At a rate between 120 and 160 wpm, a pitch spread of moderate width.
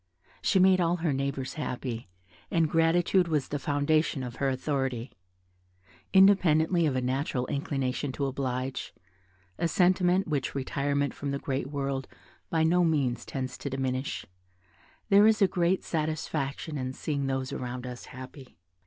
Yes: average, 145 wpm; average, 3.8 semitones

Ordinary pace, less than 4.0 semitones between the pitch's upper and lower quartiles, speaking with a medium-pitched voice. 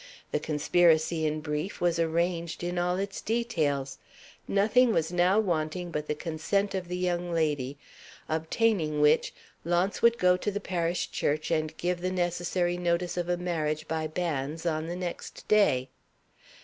Yes: average, 160 wpm; narrow, 2.5 semitones; medium, 175 Hz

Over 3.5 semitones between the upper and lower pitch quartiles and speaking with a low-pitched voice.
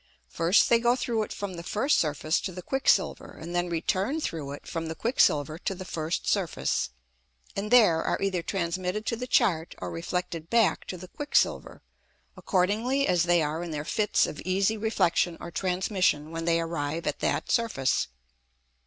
No: average, 4.4 semitones; medium, 180 Hz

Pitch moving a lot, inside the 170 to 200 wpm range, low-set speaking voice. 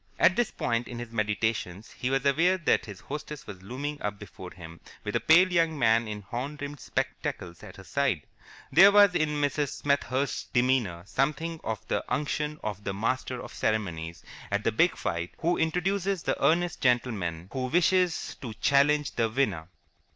Yes: wide, 6.5 semitones; average, 175 wpm; low, 130 Hz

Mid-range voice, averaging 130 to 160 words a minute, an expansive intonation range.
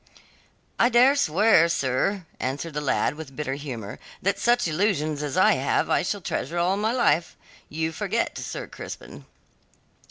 Yes: medium, 165 Hz; average, 155 wpm; wide, 5.9 semitones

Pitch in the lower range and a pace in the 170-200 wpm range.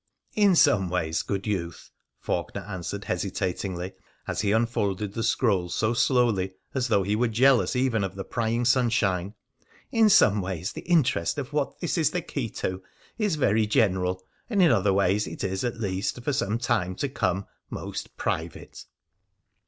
Yes: low, 105 Hz; average, 175 wpm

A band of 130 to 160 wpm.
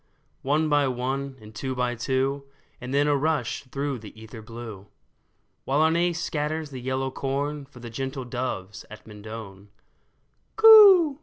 Yes: average, 155 wpm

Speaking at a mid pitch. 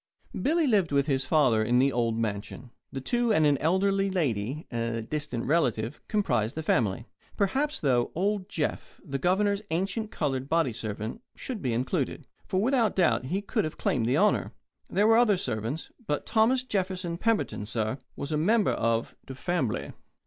Yes: medium, 155 Hz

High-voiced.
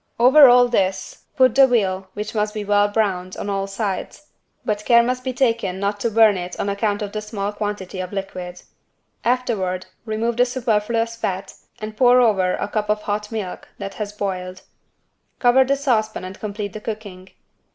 Yes: high, 210 Hz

